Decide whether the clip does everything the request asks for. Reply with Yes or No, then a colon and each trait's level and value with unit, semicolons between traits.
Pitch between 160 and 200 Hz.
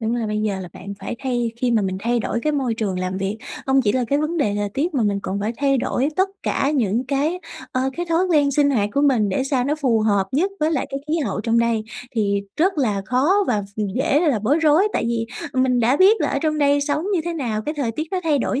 No: very high, 255 Hz